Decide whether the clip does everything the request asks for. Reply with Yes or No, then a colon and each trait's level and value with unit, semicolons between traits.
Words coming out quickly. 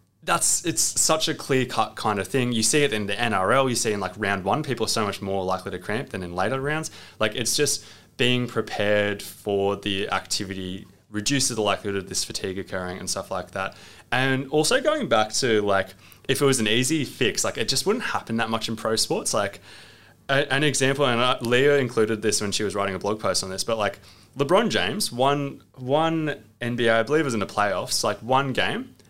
Yes: fast, 220 wpm